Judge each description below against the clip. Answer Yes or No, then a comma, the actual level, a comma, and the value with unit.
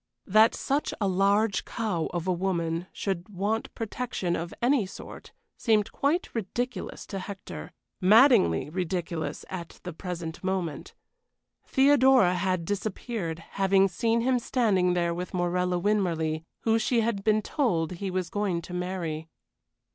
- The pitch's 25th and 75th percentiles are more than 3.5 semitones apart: Yes, average, 4.1 semitones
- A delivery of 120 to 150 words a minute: Yes, average, 140 wpm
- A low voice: No, high, 190 Hz